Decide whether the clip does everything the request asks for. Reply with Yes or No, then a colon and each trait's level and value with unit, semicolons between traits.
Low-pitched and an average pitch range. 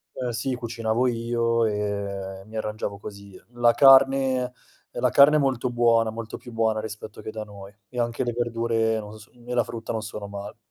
No: low, 115 Hz; narrow, 2.0 semitones